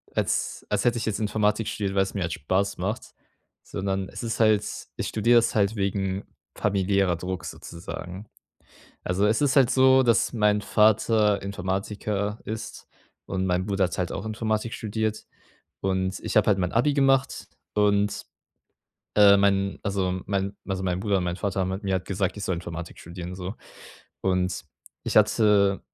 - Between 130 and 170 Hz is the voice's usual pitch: No, low, 100 Hz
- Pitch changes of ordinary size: No, narrow, 2.3 semitones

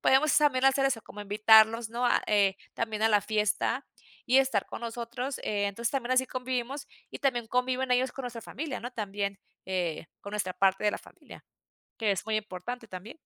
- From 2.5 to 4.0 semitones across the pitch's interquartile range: Yes, average, 3.7 semitones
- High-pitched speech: Yes, high, 230 Hz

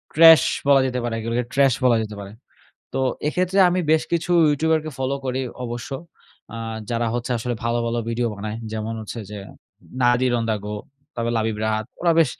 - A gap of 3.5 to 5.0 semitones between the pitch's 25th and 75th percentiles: Yes, average, 3.8 semitones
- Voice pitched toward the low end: Yes, low, 120 Hz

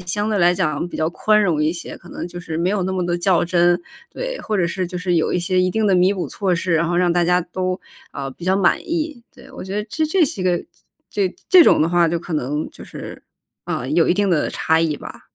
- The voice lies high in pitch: No, medium, 180 Hz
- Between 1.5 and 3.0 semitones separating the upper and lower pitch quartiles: Yes, average, 2.7 semitones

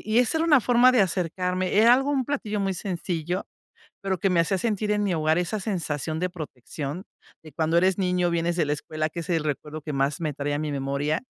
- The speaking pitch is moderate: Yes, medium, 175 Hz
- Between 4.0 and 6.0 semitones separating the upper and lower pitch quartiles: Yes, average, 4.4 semitones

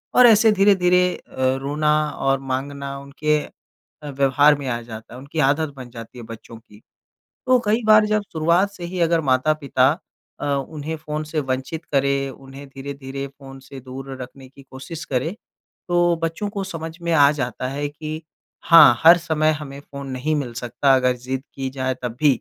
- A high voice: No, medium, 140 Hz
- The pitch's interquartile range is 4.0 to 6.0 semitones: No, average, 3.4 semitones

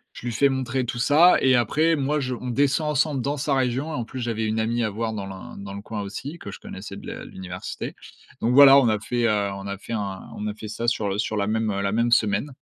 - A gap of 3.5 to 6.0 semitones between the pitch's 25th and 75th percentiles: Yes, average, 4.3 semitones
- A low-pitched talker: Yes, low, 115 Hz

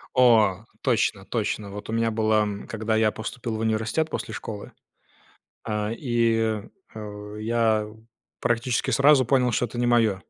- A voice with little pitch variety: Yes, narrow, 1.8 semitones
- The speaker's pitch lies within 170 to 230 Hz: No, low, 110 Hz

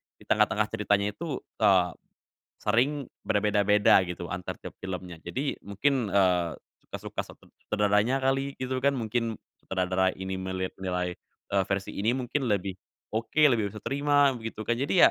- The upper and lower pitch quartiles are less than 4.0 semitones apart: No, average, 5.3 semitones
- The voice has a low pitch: Yes, low, 105 Hz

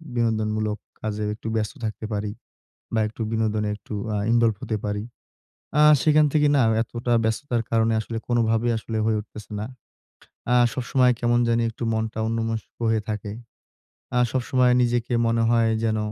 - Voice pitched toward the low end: Yes, low, 115 Hz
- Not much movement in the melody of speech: Yes, narrow, 1.7 semitones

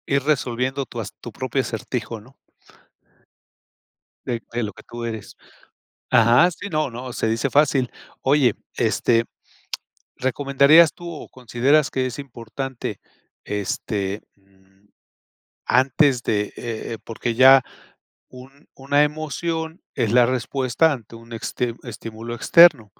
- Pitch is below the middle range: Yes, low, 125 Hz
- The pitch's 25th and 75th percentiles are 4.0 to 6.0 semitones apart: No, average, 3.4 semitones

